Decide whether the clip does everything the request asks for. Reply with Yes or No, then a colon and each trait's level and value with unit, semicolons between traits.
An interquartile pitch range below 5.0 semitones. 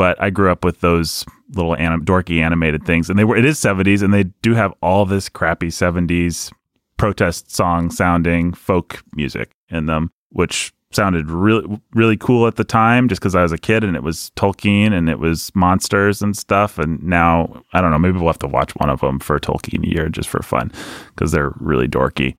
Yes: average, 3.4 semitones